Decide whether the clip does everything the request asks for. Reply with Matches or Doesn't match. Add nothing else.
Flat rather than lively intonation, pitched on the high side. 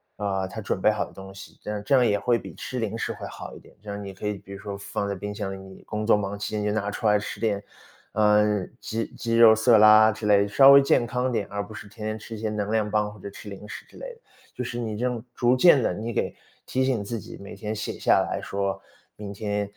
Doesn't match